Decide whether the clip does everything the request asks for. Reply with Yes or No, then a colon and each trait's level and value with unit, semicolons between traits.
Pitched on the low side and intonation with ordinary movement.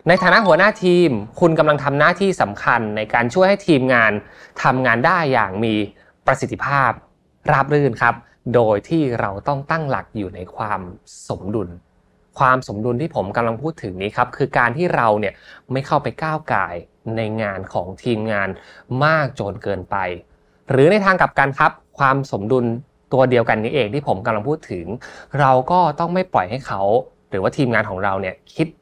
No: low, 125 Hz; wide, 6.4 semitones